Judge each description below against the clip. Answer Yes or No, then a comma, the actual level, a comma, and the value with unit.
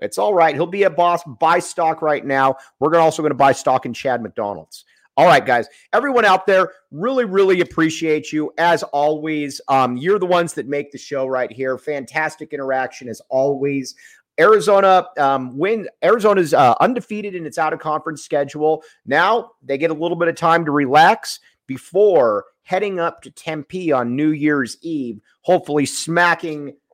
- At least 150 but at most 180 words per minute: Yes, average, 170 wpm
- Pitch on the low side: No, medium, 155 Hz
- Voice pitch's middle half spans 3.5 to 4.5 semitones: Yes, average, 3.8 semitones